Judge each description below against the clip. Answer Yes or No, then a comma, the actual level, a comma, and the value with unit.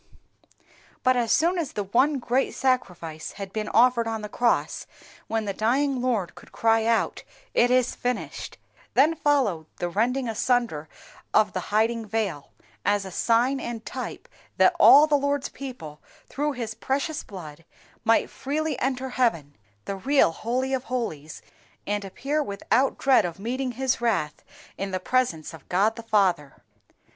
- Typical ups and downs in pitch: Yes, average, 4.8 semitones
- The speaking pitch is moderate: No, high, 230 Hz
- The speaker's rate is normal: Yes, average, 155 wpm